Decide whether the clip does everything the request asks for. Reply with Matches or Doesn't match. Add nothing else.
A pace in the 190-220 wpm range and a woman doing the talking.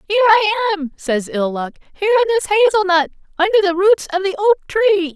Matches